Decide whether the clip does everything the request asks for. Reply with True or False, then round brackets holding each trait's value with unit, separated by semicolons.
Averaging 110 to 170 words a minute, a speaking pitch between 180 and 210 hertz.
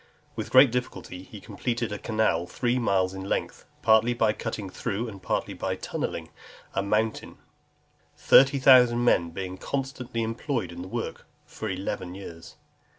False (150 wpm; 110 Hz)